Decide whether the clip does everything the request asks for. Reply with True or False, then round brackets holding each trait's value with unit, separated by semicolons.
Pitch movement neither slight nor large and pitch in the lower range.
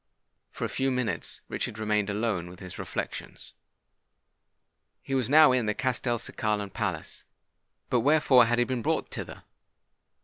True (3.5 semitones; 120 Hz)